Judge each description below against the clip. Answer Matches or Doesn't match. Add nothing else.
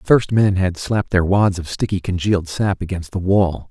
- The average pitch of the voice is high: Doesn't match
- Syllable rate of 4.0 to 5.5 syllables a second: Matches